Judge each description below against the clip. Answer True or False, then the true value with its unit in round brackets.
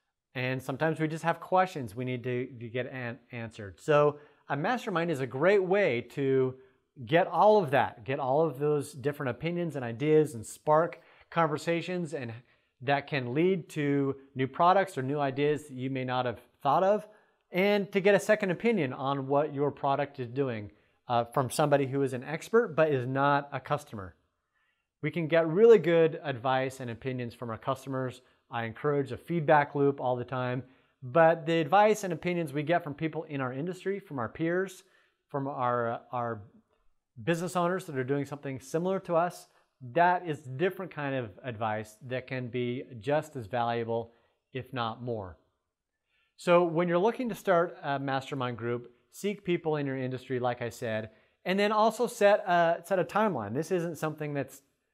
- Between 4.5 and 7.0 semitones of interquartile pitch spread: True (5.1 semitones)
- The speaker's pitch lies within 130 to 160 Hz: True (140 Hz)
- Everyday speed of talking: True (180 wpm)